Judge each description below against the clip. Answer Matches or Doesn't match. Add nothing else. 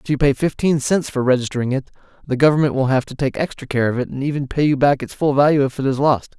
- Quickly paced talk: Matches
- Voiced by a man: Matches